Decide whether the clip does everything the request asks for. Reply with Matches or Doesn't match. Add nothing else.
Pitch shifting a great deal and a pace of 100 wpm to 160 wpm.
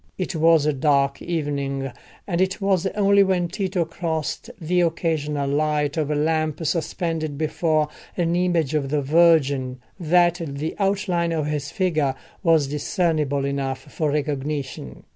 Doesn't match